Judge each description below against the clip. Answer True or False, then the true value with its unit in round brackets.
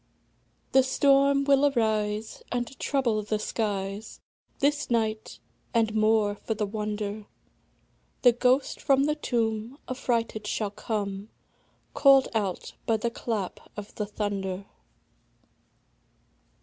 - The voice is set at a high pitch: True (220 Hz)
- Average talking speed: False (110 wpm)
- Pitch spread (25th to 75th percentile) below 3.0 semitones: False (3.5 semitones)